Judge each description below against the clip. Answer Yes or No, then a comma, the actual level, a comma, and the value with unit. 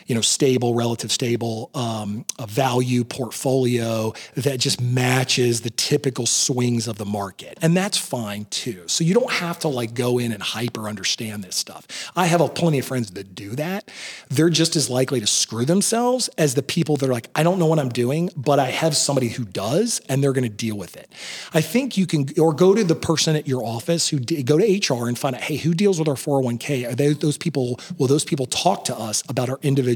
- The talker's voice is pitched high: No, low, 135 Hz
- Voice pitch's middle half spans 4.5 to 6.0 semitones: Yes, average, 5.0 semitones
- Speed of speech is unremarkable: No, fast, 230 wpm